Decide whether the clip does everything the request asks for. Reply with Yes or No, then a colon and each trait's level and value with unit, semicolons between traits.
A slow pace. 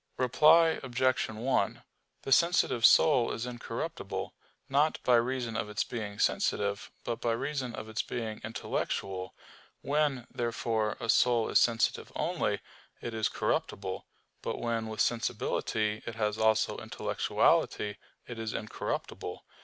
Yes: slow, 130 wpm